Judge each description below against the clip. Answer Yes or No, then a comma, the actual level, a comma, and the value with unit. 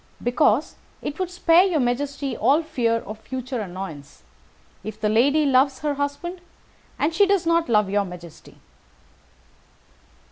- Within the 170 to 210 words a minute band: No, slow, 135 wpm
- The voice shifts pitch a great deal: Yes, wide, 6.7 semitones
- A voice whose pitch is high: Yes, very high, 260 Hz